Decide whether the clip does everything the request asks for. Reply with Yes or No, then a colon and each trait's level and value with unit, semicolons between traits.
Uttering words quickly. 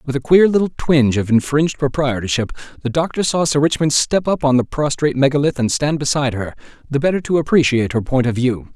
Yes: fast, 210 wpm